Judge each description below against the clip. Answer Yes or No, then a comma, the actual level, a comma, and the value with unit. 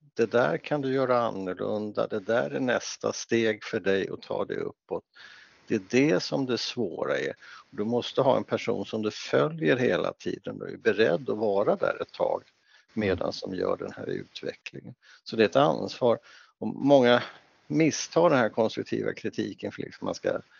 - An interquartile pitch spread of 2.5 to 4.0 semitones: No, average, 5.2 semitones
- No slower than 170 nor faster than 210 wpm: Yes, average, 190 wpm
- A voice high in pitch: No, low, 120 Hz